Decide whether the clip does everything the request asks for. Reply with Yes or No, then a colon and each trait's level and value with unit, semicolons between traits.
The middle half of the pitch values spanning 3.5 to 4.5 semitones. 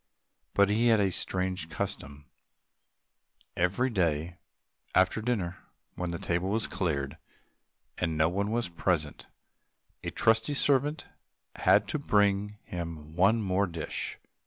Yes: average, 4.2 semitones